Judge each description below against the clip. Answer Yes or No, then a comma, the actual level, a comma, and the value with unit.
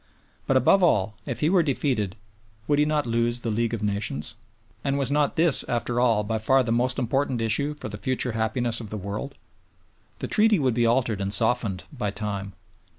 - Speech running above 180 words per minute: Yes, average, 200 wpm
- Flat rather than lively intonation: No, average, 4.1 semitones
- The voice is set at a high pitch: No, low, 120 Hz